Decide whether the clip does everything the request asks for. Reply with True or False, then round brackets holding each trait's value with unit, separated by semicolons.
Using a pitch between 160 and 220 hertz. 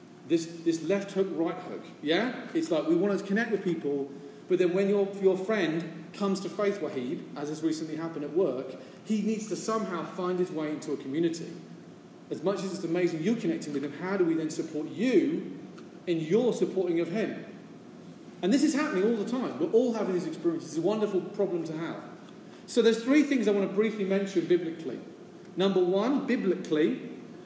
True (185 Hz)